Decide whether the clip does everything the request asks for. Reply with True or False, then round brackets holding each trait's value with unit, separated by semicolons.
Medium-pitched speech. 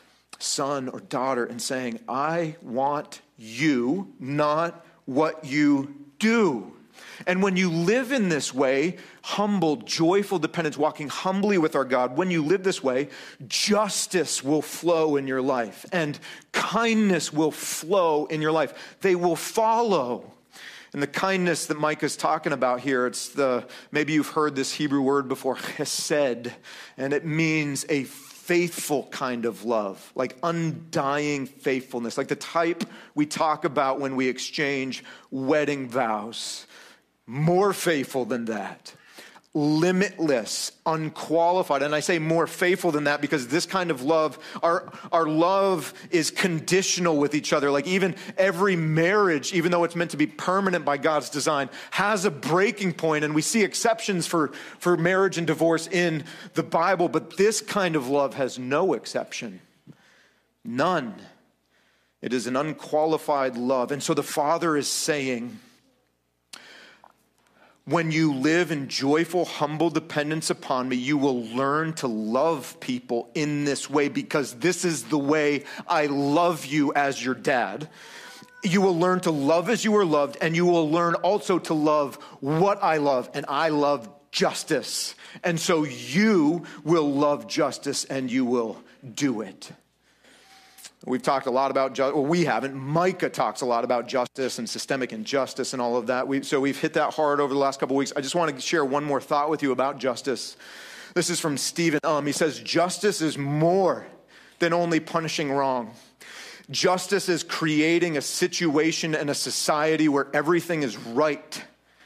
True (155 Hz)